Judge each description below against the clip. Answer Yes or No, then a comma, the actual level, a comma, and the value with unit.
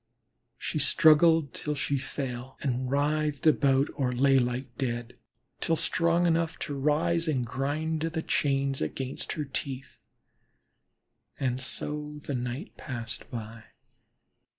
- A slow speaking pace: Yes, slow, 130 wpm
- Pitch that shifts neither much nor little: Yes, average, 3.1 semitones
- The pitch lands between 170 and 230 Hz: No, medium, 140 Hz